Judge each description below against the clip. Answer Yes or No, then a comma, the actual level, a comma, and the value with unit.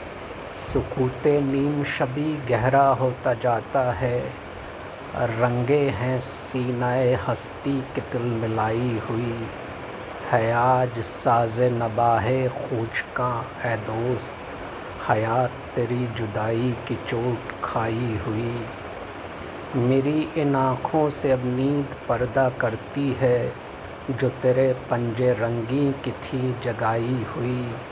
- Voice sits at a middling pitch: No, low, 125 Hz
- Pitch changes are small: Yes, narrow, 2.2 semitones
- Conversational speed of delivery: No, slow, 95 wpm